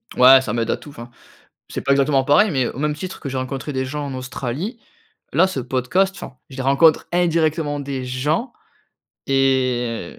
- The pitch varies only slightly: No, average, 3.1 semitones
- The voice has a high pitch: No, low, 135 Hz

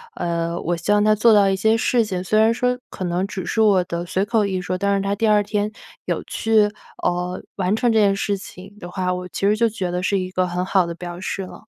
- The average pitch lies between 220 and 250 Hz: No, high, 195 Hz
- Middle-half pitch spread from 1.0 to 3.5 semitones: Yes, average, 2.7 semitones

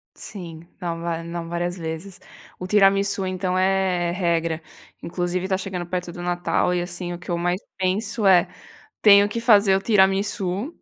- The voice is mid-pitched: Yes, medium, 180 Hz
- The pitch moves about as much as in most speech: No, narrow, 2.0 semitones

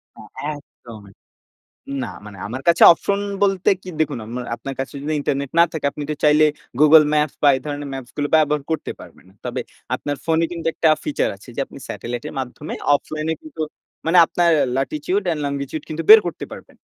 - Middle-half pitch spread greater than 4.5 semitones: No, average, 2.8 semitones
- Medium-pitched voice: Yes, medium, 150 Hz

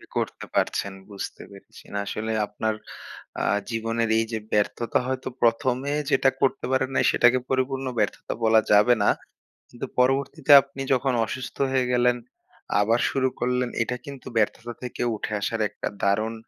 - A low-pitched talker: Yes, low, 120 Hz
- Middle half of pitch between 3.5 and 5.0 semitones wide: No, average, 2.8 semitones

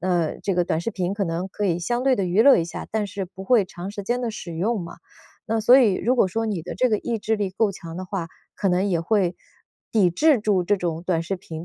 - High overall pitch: Yes, high, 195 Hz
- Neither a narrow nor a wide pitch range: Yes, average, 3.9 semitones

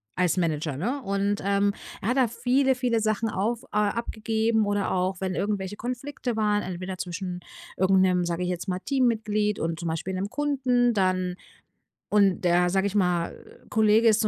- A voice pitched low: No, high, 200 Hz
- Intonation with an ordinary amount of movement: Yes, average, 3.5 semitones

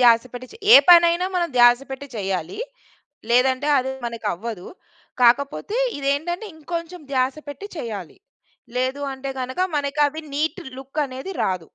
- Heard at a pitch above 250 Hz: Yes, very high, 265 Hz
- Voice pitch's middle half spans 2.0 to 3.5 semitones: No, average, 4.6 semitones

